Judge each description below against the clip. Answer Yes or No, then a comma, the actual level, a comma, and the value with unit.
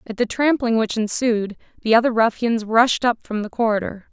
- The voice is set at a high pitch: Yes, high, 225 Hz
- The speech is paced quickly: No, average, 190 wpm